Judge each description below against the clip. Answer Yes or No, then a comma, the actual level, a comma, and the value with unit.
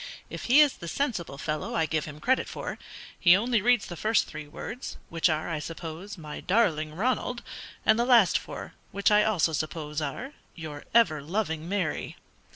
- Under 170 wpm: No, average, 180 wpm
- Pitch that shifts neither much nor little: No, wide, 6.2 semitones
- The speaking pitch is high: No, medium, 175 Hz